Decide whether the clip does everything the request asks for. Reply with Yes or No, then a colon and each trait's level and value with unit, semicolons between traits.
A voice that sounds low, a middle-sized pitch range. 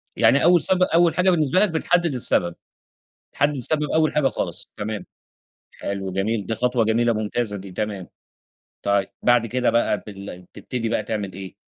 No: low, 115 Hz; wide, 6.8 semitones